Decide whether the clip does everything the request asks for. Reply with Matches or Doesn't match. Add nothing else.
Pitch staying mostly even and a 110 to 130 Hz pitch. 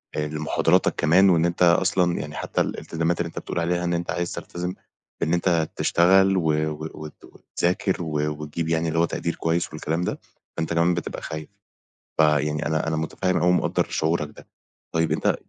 Doesn't match